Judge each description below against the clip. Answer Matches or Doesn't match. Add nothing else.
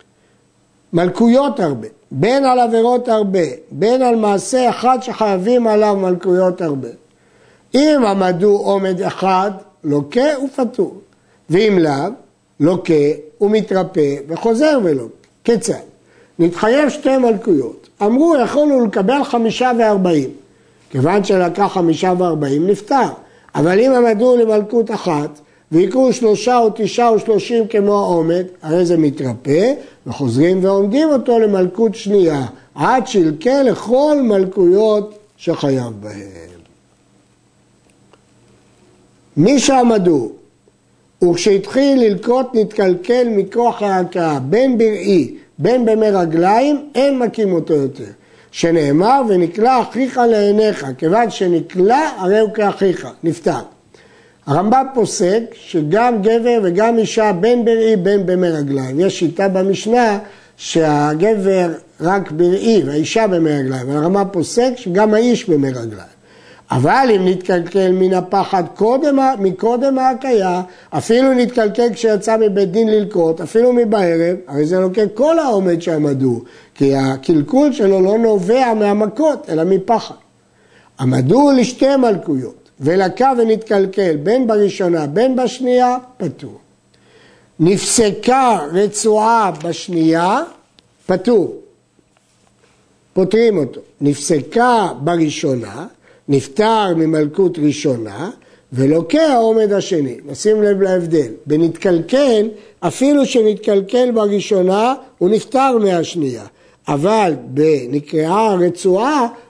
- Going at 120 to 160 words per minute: Doesn't match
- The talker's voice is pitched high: Matches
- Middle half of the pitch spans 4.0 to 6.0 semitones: Matches